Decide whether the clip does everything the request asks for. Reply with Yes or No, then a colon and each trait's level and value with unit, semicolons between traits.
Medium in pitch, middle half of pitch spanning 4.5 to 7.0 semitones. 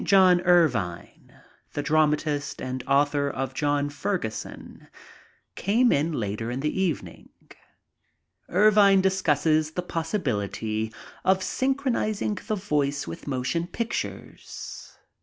Yes: medium, 155 Hz; wide, 5.5 semitones